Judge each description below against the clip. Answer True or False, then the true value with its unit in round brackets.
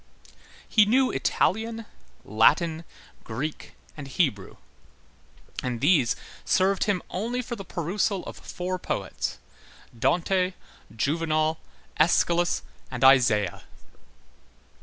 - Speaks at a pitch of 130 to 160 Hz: False (170 Hz)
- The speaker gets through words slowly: True (95 wpm)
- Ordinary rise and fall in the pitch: False (6.1 semitones)